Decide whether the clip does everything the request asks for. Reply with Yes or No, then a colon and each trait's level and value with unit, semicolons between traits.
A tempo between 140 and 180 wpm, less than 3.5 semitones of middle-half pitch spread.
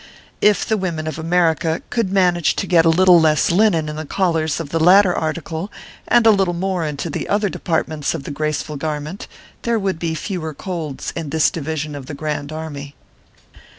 No: average, 190 wpm; average, 3.1 semitones